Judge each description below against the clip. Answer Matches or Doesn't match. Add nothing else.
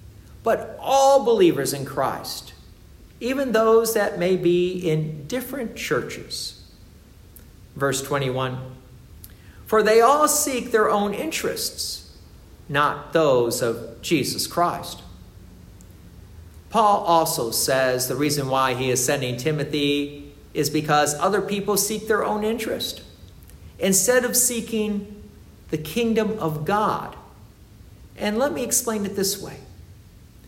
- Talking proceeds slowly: Matches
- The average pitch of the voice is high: Doesn't match